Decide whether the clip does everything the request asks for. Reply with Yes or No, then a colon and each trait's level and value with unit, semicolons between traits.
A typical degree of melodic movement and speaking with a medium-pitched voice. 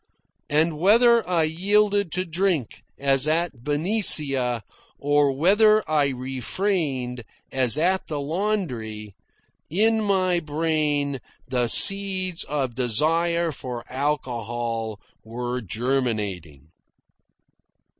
No: wide, 6.5 semitones; medium, 145 Hz